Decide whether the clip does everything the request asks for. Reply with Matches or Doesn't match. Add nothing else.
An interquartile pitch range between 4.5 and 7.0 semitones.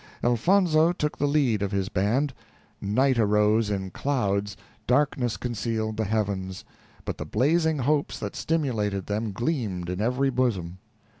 Matches